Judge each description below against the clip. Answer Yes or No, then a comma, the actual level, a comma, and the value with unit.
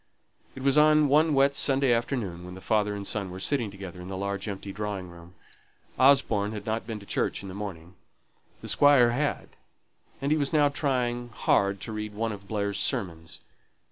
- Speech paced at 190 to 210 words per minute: Yes, average, 195 wpm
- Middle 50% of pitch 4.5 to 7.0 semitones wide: Yes, wide, 5.5 semitones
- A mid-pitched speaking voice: No, low, 105 Hz